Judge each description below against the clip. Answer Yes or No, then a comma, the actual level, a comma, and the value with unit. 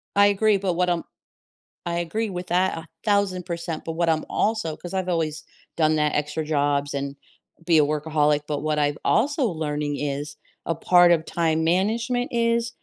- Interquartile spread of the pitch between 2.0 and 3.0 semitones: No, average, 3.9 semitones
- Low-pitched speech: No, medium, 165 Hz